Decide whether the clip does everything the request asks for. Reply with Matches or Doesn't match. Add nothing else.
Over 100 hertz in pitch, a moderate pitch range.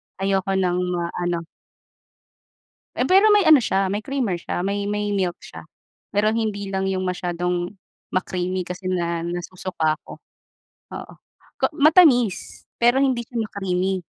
Matches